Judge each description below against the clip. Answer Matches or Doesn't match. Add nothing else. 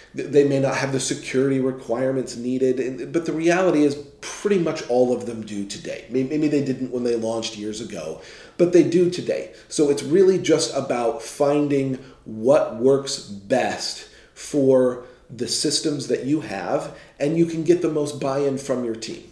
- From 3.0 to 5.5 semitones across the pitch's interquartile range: Matches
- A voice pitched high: Doesn't match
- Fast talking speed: Doesn't match